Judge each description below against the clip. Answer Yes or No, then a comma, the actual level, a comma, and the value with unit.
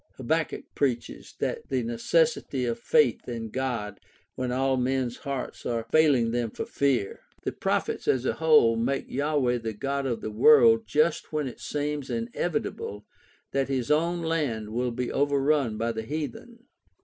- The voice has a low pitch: Yes, low, 130 Hz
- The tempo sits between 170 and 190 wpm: No, average, 155 wpm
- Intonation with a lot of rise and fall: No, average, 4.2 semitones